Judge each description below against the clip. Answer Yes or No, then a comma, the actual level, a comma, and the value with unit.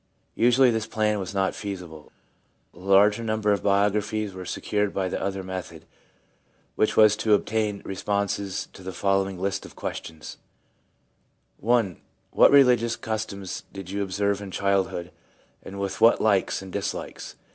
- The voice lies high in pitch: No, low, 100 Hz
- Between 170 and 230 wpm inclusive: No, average, 160 wpm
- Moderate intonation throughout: No, narrow, 2.0 semitones